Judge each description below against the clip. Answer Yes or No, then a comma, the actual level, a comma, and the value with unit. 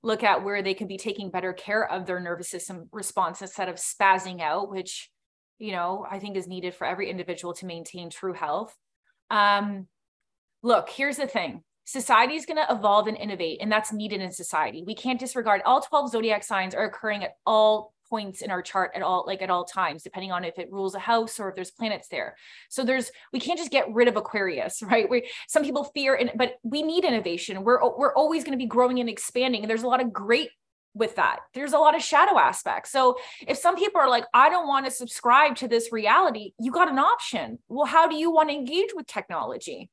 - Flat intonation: No, average, 5.2 semitones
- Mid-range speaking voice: No, high, 220 Hz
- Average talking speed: No, fast, 225 wpm